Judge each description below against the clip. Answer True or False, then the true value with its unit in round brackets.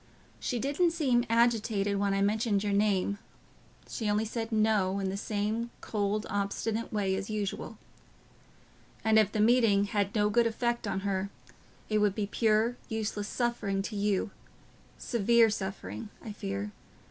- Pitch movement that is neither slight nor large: False (2.2 semitones)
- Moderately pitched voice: False (210 Hz)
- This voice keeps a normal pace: True (145 wpm)